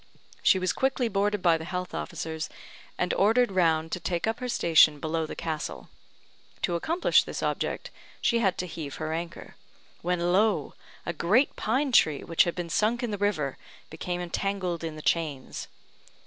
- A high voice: No, medium, 175 Hz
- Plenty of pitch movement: No, average, 4.2 semitones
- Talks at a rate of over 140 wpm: Yes, average, 175 wpm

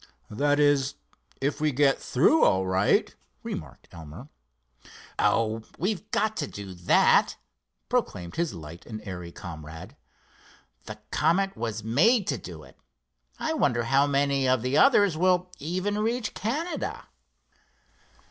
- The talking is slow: Yes, slow, 130 wpm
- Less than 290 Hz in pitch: Yes, medium, 140 Hz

